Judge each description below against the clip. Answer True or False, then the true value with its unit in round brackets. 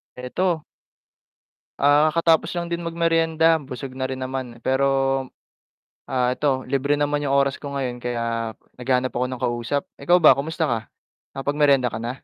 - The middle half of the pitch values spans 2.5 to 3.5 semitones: True (3.0 semitones)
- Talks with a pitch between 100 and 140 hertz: True (135 Hz)